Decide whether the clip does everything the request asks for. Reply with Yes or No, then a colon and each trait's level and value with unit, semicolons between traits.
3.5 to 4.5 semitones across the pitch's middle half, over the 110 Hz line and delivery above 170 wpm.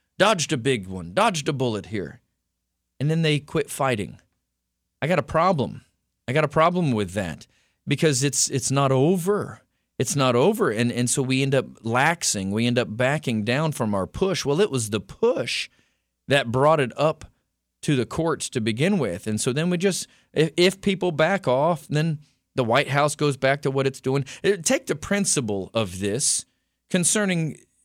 No: average, 5.2 semitones; medium, 140 Hz; average, 185 wpm